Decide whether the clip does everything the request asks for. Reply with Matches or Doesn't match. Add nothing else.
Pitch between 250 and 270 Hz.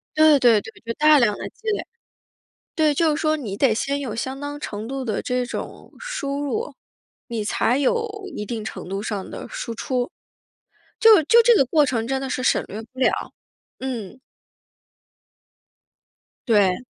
Matches